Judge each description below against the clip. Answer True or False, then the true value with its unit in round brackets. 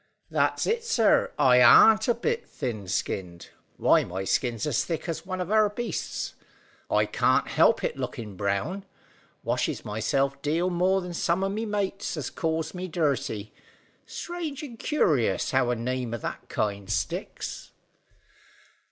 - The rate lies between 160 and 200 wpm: False (150 wpm)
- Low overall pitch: False (160 Hz)